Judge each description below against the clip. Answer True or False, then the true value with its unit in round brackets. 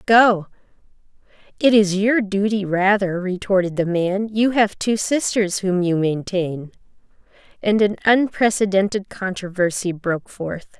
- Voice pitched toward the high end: True (195 Hz)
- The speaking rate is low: True (110 wpm)